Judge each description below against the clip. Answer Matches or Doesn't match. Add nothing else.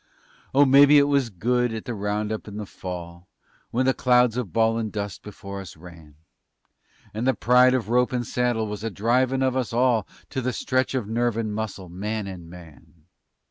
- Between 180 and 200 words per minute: Matches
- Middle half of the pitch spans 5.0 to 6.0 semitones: Doesn't match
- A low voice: Matches